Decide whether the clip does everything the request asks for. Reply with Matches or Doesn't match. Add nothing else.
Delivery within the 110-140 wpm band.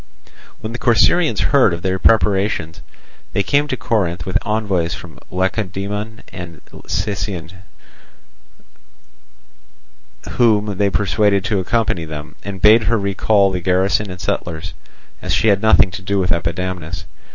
Matches